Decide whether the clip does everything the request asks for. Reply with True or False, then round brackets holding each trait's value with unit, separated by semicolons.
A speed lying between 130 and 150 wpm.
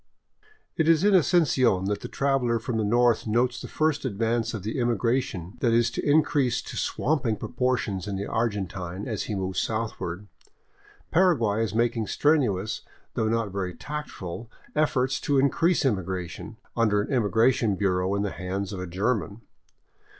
False (160 wpm)